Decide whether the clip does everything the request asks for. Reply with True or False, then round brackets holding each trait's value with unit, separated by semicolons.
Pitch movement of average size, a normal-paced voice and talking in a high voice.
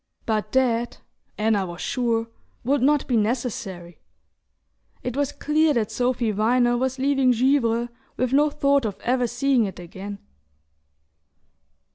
False (3.3 semitones; 130 wpm; 245 Hz)